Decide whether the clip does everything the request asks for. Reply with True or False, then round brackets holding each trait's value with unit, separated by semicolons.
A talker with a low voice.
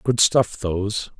True (105 Hz)